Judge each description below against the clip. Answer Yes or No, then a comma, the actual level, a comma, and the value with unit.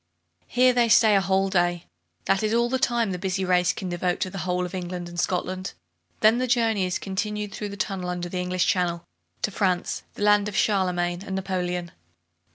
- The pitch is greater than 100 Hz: Yes, high, 190 Hz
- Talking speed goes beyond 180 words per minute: Yes, fast, 205 wpm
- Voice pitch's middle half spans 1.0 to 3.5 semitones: Yes, average, 2.7 semitones